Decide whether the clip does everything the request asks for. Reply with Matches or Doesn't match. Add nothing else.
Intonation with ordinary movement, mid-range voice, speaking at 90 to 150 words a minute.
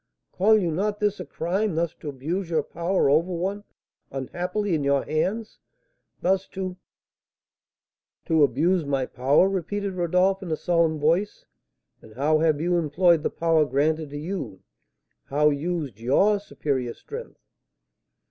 Matches